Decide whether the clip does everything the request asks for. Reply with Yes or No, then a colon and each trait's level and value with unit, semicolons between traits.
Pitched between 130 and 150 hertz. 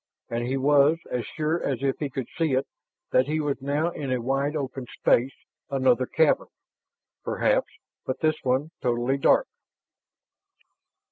Yes: low, 135 Hz